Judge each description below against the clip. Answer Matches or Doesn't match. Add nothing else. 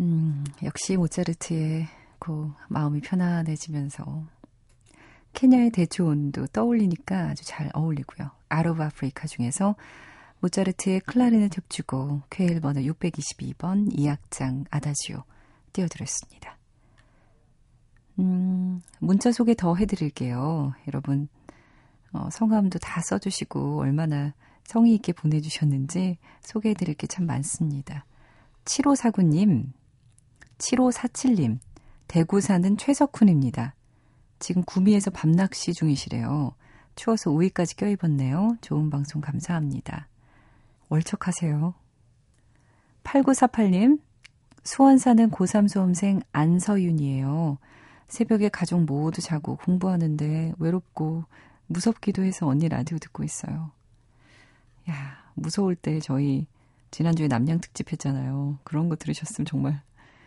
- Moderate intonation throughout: Matches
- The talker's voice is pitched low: Doesn't match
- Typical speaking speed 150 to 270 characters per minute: Matches